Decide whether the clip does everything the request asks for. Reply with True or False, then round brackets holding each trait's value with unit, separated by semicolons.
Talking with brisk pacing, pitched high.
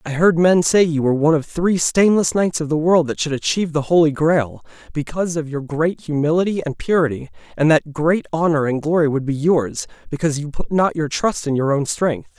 False (225 wpm; 155 Hz)